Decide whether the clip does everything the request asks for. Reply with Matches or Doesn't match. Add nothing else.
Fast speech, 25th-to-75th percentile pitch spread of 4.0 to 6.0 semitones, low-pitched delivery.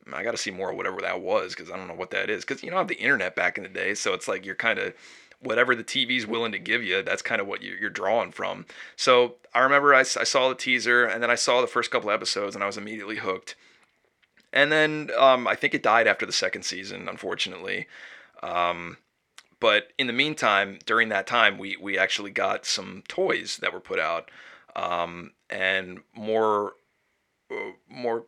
Matches